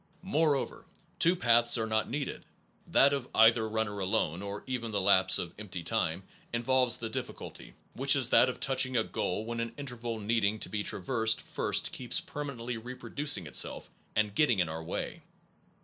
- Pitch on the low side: Yes, low, 115 Hz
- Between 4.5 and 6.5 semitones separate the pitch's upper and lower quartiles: No, average, 3.8 semitones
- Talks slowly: No, average, 175 wpm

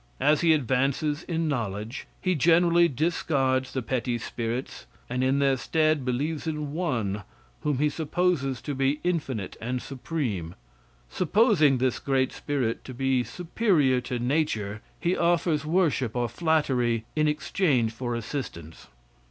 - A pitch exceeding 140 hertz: No, low, 135 Hz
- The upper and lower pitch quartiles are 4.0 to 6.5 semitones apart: Yes, average, 4.5 semitones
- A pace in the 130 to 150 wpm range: Yes, slow, 135 wpm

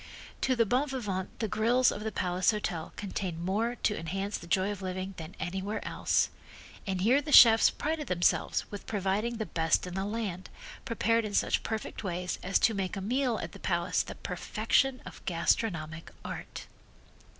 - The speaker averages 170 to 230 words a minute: Yes, average, 180 wpm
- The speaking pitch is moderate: No, high, 200 Hz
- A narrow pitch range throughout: No, average, 3.9 semitones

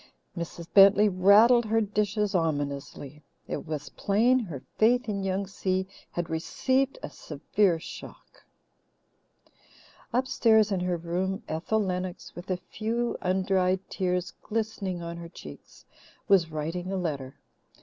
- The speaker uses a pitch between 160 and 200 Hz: Yes, high, 190 Hz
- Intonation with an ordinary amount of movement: Yes, average, 3.8 semitones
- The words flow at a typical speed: No, slow, 130 wpm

